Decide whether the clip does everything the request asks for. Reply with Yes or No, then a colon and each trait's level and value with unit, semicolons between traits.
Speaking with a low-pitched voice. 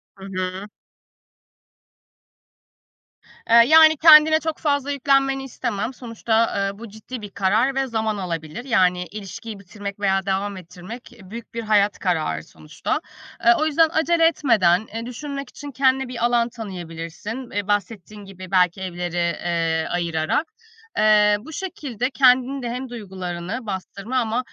No: high, 215 Hz